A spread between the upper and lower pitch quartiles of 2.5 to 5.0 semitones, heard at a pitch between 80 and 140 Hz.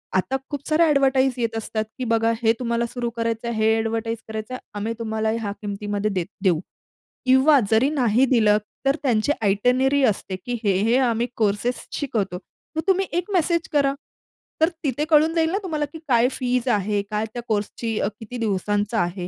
No: average, 3.9 semitones; high, 230 Hz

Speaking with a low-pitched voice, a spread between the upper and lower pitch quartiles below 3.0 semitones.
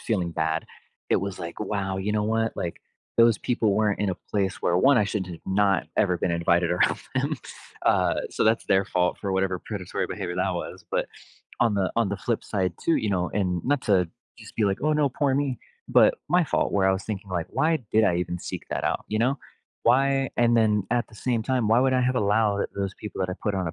No: low, 105 Hz; average, 4.1 semitones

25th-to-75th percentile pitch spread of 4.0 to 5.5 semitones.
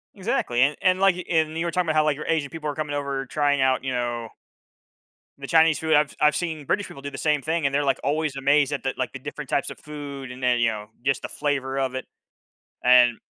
No: average, 2.8 semitones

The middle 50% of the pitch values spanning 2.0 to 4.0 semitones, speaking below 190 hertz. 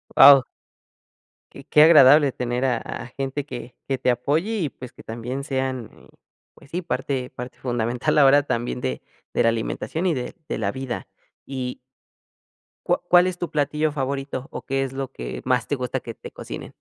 Yes: narrow, 2.6 semitones; low, 135 Hz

